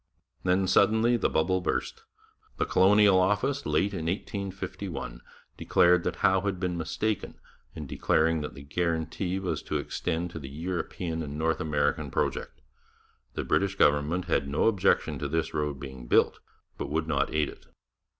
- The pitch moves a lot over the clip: No, average, 4.0 semitones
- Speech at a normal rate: Yes, average, 160 wpm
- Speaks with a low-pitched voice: Yes, very low, 85 Hz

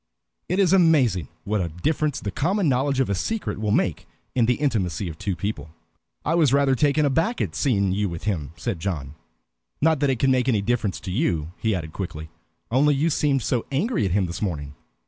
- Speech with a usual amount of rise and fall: No, wide, 8.0 semitones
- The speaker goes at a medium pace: No, fast, 210 wpm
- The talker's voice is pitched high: No, low, 115 Hz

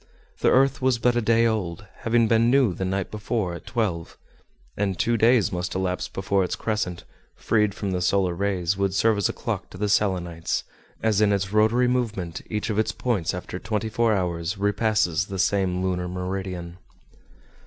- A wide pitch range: No, average, 3.4 semitones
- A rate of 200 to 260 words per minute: No, average, 185 wpm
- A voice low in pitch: Yes, low, 100 Hz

